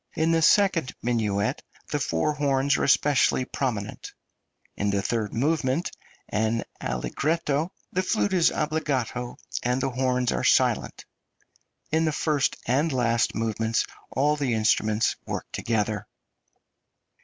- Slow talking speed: Yes, slow, 125 wpm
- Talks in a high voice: No, low, 130 Hz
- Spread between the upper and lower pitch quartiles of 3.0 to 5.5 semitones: Yes, average, 5.1 semitones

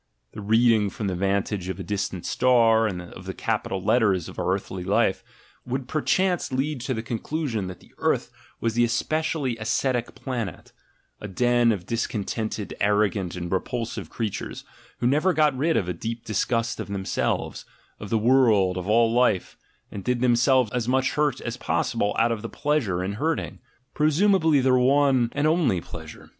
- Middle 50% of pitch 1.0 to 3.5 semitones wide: No, average, 4.6 semitones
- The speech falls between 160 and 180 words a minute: Yes, average, 170 wpm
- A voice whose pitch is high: No, low, 115 Hz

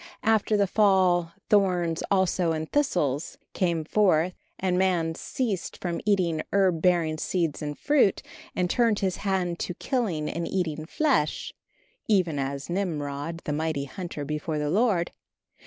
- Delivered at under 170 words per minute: Yes, average, 140 wpm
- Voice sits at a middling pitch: Yes, medium, 175 Hz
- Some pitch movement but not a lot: Yes, average, 3.6 semitones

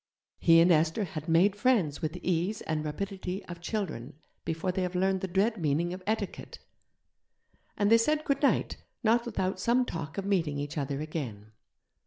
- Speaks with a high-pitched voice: No, medium, 180 Hz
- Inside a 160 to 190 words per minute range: Yes, average, 180 wpm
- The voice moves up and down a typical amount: Yes, average, 4.5 semitones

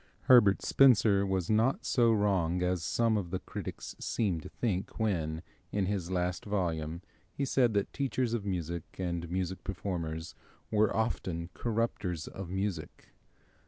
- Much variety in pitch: No, average, 4.0 semitones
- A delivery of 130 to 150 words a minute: Yes, average, 145 wpm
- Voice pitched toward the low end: Yes, very low, 95 Hz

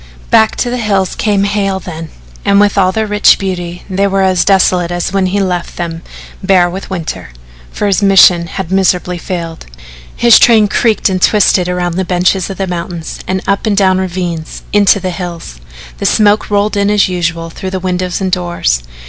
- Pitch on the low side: No, medium, 185 Hz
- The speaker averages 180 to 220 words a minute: Yes, average, 190 wpm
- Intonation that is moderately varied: No, narrow, 2.2 semitones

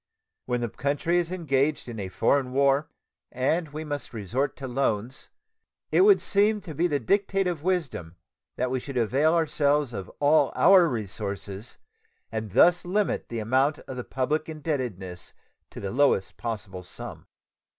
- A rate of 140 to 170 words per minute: Yes, average, 160 wpm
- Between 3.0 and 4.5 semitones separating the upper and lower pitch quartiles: No, wide, 5.6 semitones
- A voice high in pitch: No, medium, 140 Hz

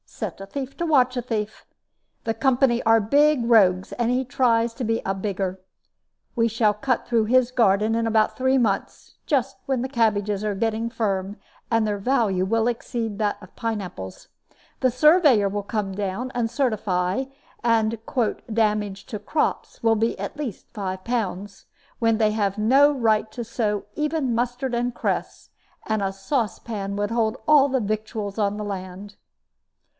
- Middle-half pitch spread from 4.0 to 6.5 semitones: No, average, 3.2 semitones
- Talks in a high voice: Yes, high, 225 Hz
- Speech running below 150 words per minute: No, average, 170 wpm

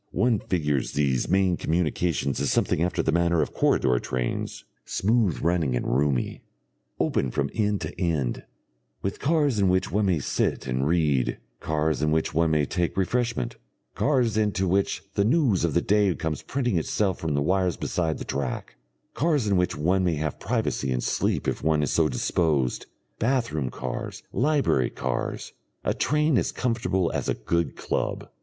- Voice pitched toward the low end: Yes, very low, 85 Hz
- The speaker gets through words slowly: No, average, 175 wpm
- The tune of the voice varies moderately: No, wide, 5.8 semitones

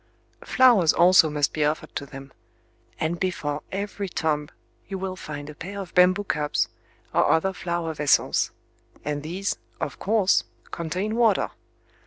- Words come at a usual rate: Yes, average, 145 wpm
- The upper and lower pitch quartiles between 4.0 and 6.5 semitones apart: Yes, average, 4.3 semitones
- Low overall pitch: No, medium, 170 Hz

